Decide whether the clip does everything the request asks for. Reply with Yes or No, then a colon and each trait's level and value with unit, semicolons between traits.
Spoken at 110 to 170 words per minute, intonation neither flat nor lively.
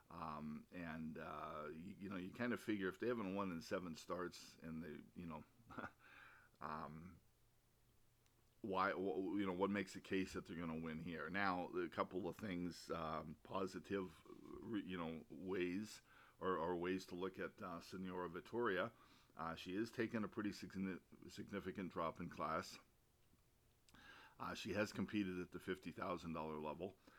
Yes: average, 160 wpm; average, 3.4 semitones